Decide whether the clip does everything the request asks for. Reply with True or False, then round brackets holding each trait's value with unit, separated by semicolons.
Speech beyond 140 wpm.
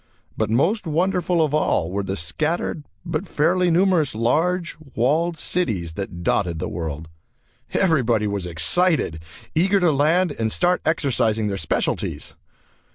False (135 wpm)